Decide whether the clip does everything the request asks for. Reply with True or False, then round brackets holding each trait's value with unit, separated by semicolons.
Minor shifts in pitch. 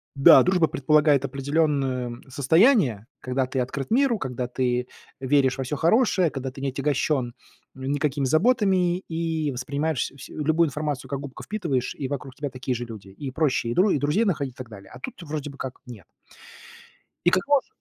False (3.8 semitones)